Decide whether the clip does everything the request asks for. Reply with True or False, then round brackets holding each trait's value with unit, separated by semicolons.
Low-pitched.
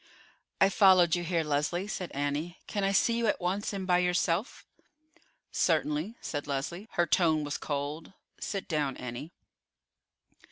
False (175 Hz)